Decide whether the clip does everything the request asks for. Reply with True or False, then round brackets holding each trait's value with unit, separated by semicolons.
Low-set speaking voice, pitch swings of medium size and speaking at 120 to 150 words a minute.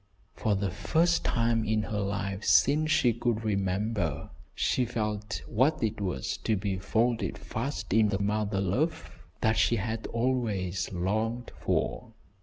True (110 Hz; 3.0 semitones; 145 wpm)